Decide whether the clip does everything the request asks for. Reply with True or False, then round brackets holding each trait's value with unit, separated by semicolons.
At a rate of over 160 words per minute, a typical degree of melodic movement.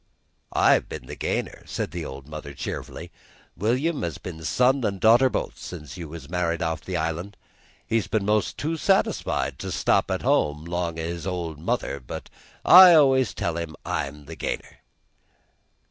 False (170 wpm; 5.8 semitones)